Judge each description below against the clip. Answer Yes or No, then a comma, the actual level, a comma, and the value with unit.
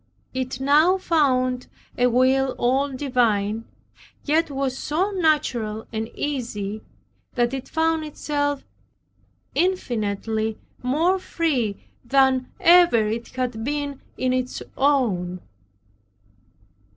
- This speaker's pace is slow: Yes, slow, 100 wpm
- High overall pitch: Yes, very high, 260 Hz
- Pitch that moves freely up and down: No, average, 4.0 semitones